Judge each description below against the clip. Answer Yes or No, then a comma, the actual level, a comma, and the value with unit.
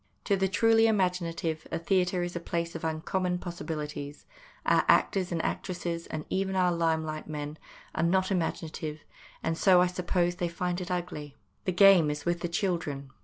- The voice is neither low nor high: Yes, medium, 175 Hz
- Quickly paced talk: No, average, 175 wpm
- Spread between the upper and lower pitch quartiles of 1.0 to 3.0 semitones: Yes, narrow, 2.4 semitones